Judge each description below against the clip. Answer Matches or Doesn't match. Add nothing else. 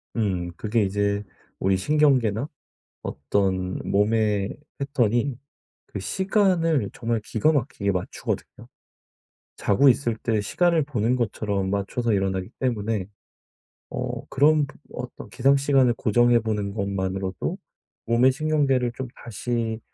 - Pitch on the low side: Matches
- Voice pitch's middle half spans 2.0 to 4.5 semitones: Doesn't match